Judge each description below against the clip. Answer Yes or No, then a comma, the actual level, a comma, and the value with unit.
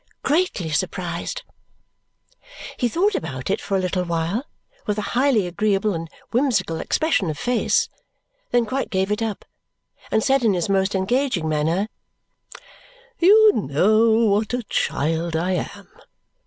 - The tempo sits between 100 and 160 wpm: Yes, average, 140 wpm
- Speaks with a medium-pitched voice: No, high, 200 Hz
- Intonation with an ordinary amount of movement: No, wide, 5.8 semitones